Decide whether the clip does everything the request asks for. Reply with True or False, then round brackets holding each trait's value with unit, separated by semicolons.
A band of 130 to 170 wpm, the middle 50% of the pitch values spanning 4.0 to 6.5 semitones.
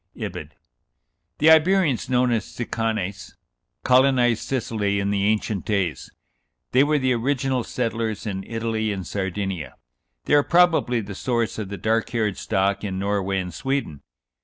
True (145 wpm; 4.3 semitones)